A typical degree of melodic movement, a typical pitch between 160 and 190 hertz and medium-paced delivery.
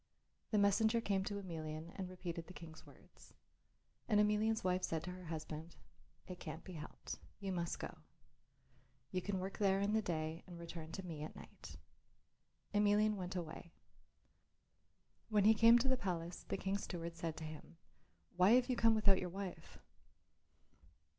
Yes: average, 3.7 semitones; medium, 185 Hz; average, 165 wpm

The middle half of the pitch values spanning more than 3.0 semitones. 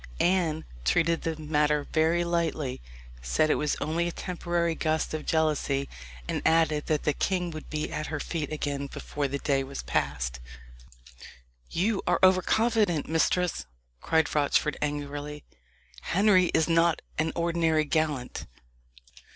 No: narrow, 2.4 semitones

